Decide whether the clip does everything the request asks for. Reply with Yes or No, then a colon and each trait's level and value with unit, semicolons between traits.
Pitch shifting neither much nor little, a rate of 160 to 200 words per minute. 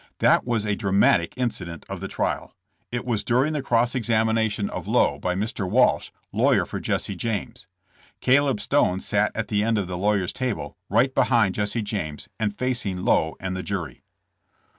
Yes: average, 3.9 semitones; average, 175 wpm